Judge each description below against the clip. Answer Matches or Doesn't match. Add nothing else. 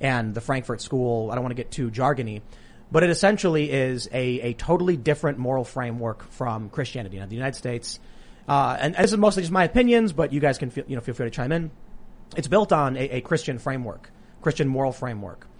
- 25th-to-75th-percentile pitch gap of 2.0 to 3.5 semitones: Doesn't match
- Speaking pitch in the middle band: Doesn't match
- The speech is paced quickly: Matches